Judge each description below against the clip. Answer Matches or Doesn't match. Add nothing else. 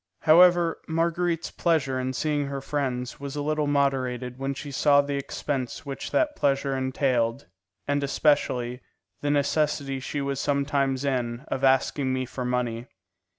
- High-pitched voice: Doesn't match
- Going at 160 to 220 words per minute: Doesn't match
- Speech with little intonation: Matches